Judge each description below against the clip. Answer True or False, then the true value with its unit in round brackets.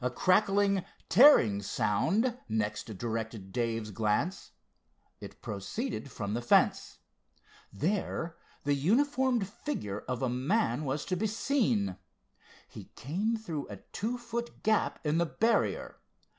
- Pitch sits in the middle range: True (155 Hz)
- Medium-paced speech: False (125 wpm)